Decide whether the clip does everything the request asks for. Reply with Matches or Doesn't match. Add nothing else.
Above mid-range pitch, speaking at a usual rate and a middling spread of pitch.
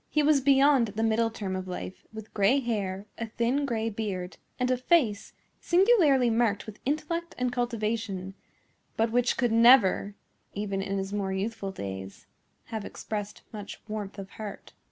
Matches